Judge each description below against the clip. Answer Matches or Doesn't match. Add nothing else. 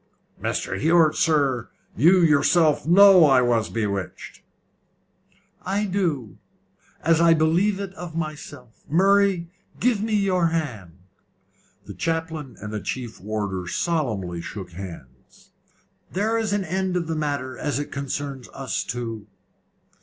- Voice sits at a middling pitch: Matches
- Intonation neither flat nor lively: Doesn't match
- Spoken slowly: Matches